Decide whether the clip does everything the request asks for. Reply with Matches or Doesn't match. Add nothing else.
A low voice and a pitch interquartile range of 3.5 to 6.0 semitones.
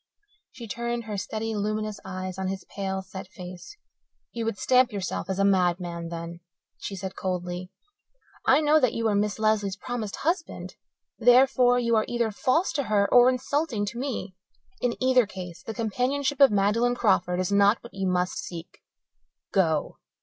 Doesn't match